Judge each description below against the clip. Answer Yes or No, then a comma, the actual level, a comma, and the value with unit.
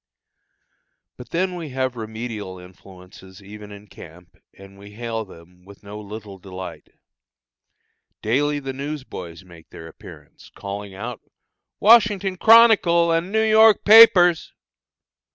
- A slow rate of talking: Yes, slow, 125 wpm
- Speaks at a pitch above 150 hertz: No, low, 110 Hz